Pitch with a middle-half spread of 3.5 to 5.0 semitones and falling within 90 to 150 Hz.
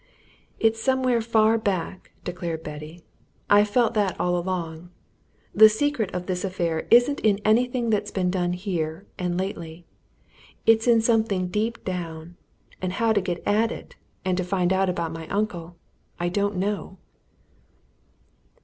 No: average, 3.8 semitones; high, 190 Hz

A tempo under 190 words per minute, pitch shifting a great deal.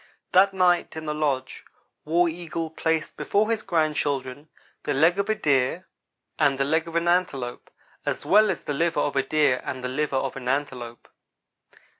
No: average, 180 wpm; average, 4.1 semitones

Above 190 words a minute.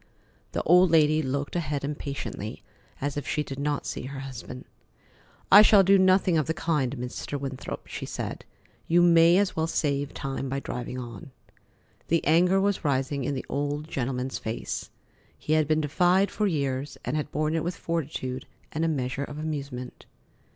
No: average, 175 wpm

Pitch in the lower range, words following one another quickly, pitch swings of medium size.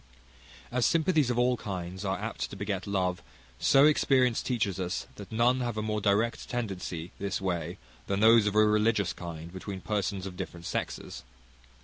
No: low, 100 Hz; average, 170 wpm; average, 4.0 semitones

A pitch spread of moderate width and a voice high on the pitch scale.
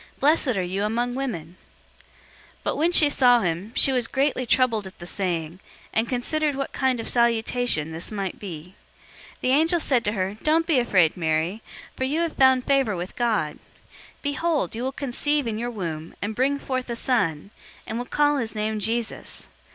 No: wide, 5.8 semitones; high, 235 Hz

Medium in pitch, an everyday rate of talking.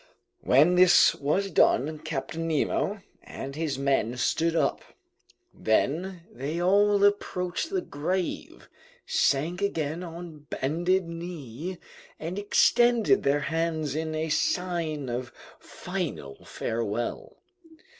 No: medium, 165 Hz; slow, 105 wpm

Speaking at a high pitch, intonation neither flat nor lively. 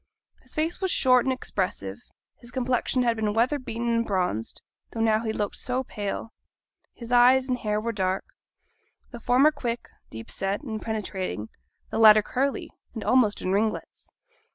Yes: high, 230 Hz; average, 3.4 semitones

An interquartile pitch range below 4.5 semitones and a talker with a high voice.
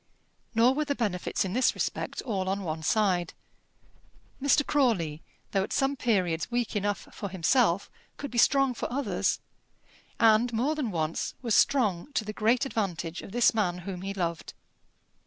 No: wide, 5.5 semitones; high, 215 Hz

